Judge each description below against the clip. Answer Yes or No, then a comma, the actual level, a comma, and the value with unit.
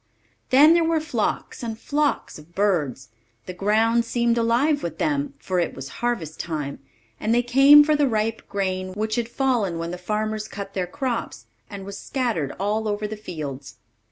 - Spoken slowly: No, average, 180 wpm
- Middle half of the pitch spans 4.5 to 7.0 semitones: Yes, average, 5.1 semitones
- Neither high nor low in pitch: No, high, 215 Hz